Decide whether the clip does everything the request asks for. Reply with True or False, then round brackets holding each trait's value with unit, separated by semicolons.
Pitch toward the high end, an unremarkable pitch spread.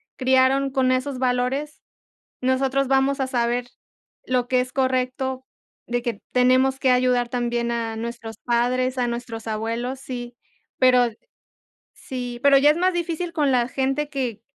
False (255 Hz; 1.8 semitones)